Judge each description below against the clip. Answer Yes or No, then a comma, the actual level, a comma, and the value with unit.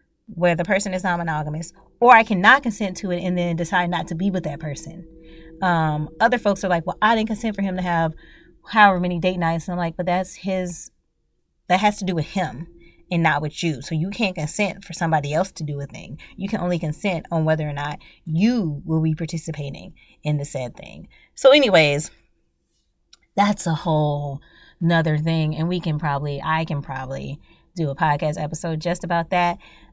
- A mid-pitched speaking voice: Yes, medium, 165 Hz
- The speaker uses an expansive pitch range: No, average, 3.3 semitones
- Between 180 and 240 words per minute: Yes, fast, 205 wpm